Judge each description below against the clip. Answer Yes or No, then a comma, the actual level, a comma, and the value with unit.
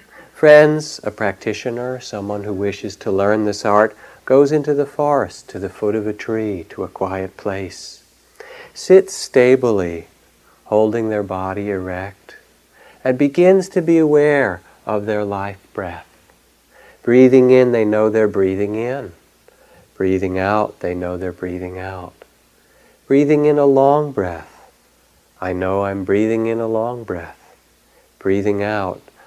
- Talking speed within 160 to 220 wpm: No, average, 140 wpm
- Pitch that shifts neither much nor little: No, wide, 5.8 semitones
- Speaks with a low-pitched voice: Yes, low, 105 Hz